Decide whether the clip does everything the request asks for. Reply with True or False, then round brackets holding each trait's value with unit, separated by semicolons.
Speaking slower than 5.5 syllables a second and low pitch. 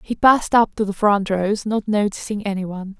False (5.3 syllables/s; 205 Hz)